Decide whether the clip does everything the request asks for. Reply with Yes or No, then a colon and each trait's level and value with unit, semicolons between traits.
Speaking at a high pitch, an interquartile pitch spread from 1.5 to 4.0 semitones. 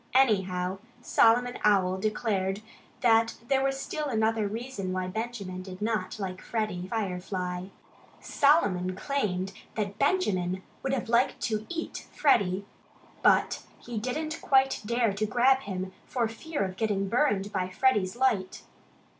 No: high, 215 Hz; average, 4.7 semitones